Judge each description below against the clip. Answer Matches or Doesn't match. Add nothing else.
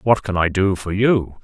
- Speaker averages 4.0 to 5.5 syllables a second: Matches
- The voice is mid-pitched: Doesn't match